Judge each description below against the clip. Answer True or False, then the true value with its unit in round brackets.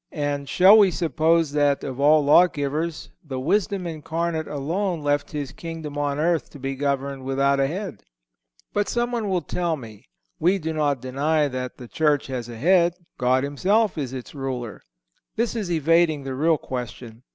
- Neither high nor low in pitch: True (150 Hz)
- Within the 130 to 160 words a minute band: False (170 wpm)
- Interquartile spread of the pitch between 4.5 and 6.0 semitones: False (3.8 semitones)